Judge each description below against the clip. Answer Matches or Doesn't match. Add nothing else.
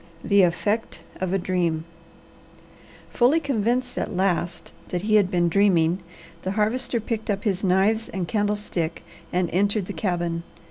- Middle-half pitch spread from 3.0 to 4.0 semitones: Matches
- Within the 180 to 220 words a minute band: Doesn't match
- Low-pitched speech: Doesn't match